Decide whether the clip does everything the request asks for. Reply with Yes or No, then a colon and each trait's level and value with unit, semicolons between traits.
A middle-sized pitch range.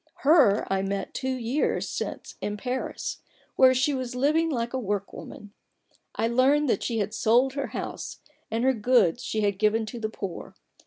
Yes: average, 3.9 semitones